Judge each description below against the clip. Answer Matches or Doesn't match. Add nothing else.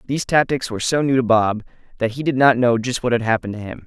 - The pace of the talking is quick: Matches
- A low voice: Matches